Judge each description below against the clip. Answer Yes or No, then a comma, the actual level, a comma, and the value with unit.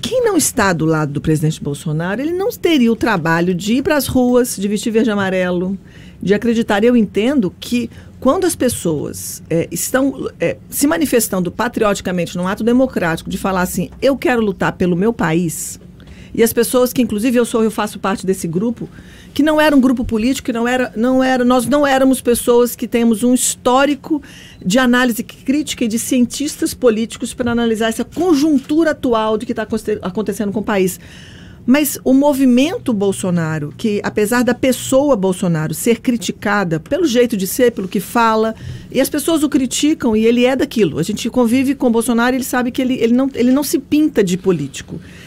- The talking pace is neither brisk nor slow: No, fast, 190 wpm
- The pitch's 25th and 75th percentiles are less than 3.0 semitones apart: No, average, 4.6 semitones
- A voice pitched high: Yes, high, 235 Hz